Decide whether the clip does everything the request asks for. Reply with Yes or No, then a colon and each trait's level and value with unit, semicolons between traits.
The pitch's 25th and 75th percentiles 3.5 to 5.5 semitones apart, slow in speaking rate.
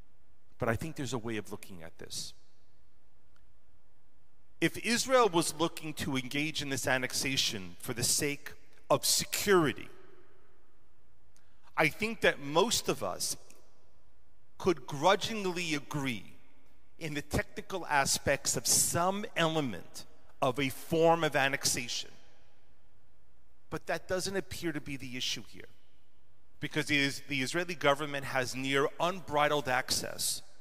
Yes: average, 4.2 semitones; slow, 120 wpm